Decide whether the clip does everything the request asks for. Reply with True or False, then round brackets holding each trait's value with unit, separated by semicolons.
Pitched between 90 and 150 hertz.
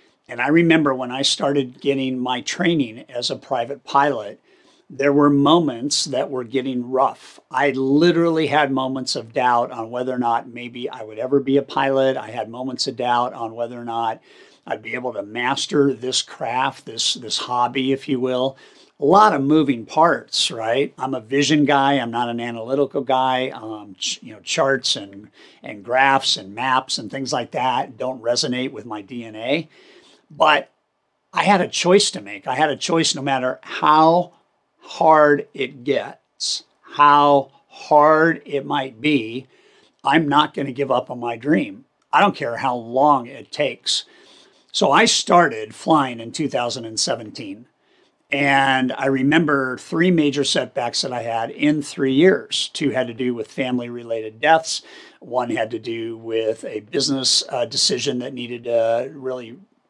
True (135 Hz)